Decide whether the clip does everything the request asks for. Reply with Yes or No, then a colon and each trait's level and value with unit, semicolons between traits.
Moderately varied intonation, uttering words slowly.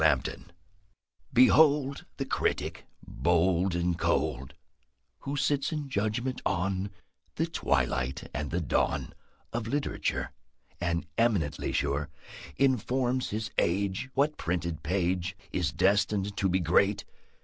No: wide, 6.5 semitones; slow, 115 wpm